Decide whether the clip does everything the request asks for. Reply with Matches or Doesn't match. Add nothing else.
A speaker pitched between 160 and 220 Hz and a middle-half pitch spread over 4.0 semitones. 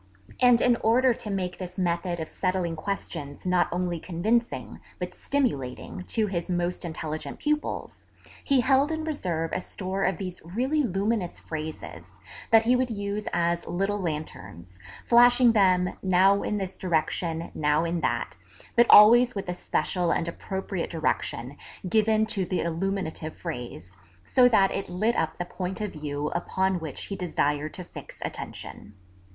Matches